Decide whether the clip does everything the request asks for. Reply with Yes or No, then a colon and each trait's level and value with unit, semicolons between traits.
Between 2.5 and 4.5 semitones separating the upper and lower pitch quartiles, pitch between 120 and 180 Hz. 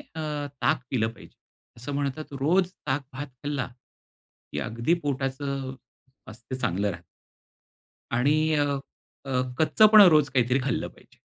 Yes: average, 2.9 semitones; low, 135 Hz